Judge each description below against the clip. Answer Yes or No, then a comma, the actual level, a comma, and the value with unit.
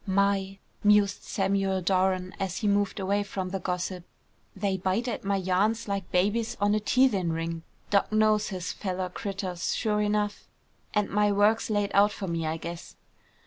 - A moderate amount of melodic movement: No, narrow, 2.0 semitones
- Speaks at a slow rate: No, average, 170 wpm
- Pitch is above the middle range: Yes, high, 200 Hz